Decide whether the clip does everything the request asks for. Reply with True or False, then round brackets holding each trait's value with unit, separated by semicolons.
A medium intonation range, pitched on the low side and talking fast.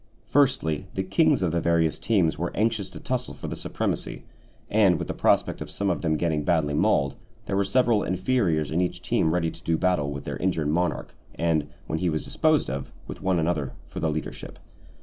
True (3.9 semitones; 85 Hz; 210 wpm)